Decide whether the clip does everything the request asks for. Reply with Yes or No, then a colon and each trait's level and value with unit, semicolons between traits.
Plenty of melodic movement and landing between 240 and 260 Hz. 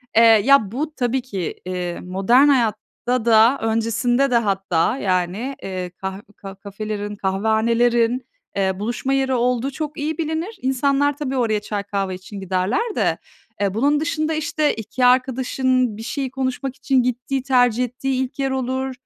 No: average, 4.5 semitones; high, 245 Hz